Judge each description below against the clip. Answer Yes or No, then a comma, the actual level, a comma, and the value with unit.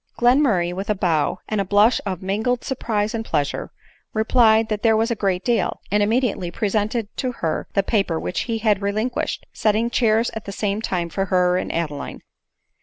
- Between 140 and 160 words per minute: No, average, 190 wpm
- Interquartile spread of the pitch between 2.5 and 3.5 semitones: Yes, average, 3.1 semitones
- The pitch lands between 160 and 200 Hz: No, high, 210 Hz